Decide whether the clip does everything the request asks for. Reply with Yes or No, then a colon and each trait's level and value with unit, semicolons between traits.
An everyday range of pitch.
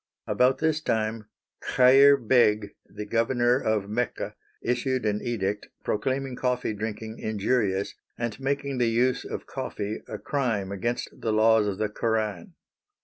Yes: average, 3.2 semitones